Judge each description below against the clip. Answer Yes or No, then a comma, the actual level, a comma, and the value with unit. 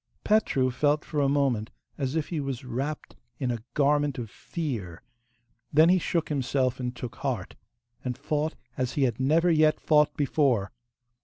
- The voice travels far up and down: No, average, 3.4 semitones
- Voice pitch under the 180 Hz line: Yes, medium, 140 Hz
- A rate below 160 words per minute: No, average, 165 wpm